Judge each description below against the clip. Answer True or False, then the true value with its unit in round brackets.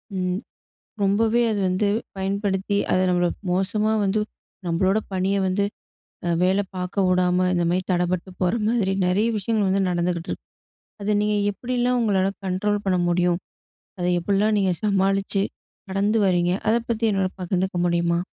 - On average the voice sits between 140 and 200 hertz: True (190 Hz)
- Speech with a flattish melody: True (2.3 semitones)